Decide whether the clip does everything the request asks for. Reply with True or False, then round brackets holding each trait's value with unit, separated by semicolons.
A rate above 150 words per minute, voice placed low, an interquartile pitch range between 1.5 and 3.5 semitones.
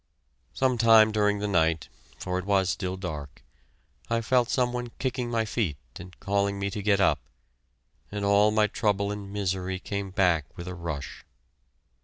True (170 wpm; 100 Hz; 2.8 semitones)